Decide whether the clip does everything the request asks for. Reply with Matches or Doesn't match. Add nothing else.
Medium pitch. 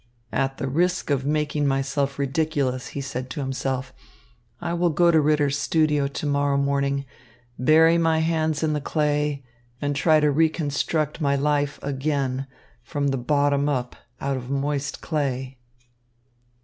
Matches